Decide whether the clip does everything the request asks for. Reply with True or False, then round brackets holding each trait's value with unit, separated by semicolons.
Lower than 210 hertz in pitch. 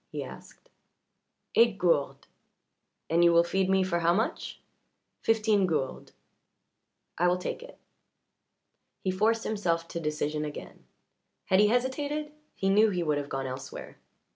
True (185 Hz)